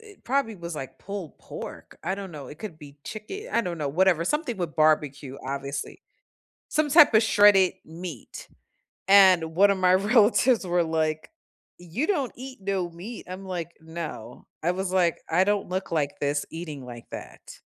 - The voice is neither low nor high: Yes, medium, 180 Hz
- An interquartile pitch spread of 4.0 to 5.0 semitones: Yes, average, 4.7 semitones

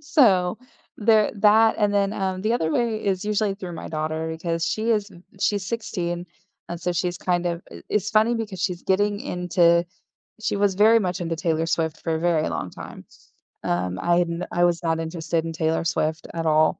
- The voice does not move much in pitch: No, average, 3.9 semitones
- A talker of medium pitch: Yes, medium, 180 Hz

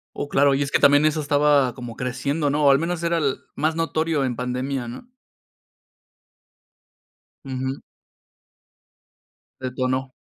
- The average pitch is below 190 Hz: Yes, medium, 140 Hz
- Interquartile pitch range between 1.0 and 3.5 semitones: Yes, average, 2.8 semitones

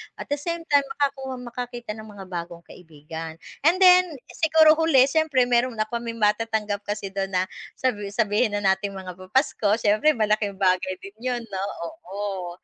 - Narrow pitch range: No, average, 5.0 semitones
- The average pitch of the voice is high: Yes, high, 215 Hz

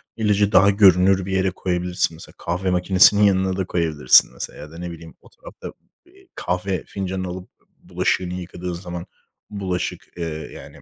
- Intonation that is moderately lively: No, narrow, 1.6 semitones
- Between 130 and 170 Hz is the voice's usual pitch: No, very low, 90 Hz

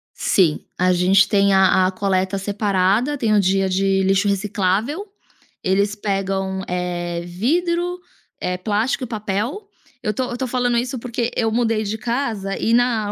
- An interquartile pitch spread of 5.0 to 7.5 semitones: No, average, 3.7 semitones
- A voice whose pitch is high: Yes, high, 205 Hz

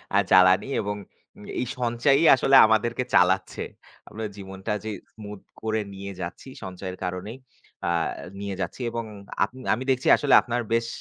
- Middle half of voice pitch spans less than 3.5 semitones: No, average, 3.8 semitones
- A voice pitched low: Yes, low, 105 Hz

